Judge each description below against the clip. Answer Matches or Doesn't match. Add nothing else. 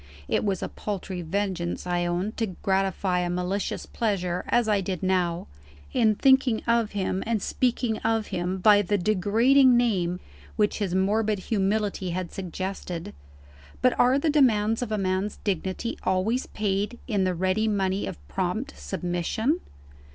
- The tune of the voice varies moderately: Matches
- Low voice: Doesn't match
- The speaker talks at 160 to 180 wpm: Doesn't match